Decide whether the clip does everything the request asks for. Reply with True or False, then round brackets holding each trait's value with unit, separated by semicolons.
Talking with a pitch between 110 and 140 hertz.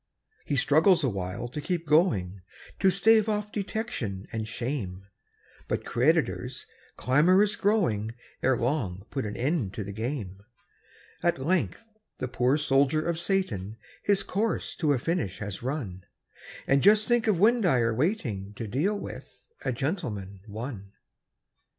True (135 Hz)